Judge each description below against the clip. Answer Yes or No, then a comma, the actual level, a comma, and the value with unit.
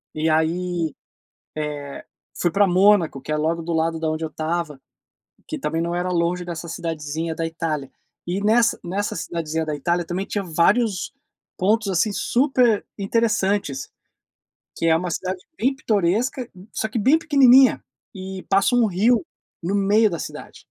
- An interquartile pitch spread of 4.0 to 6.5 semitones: Yes, average, 4.4 semitones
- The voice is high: No, medium, 180 Hz